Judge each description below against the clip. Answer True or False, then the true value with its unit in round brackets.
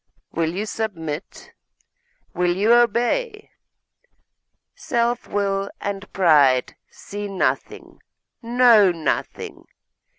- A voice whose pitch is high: True (200 Hz)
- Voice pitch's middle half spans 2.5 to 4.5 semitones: False (5.0 semitones)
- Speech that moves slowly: True (80 wpm)